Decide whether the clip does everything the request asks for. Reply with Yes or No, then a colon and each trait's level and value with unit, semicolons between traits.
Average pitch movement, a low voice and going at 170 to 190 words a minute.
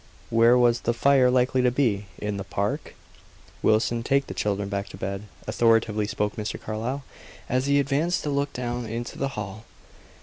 Yes: average, 3.6 semitones; low, 120 Hz; average, 175 wpm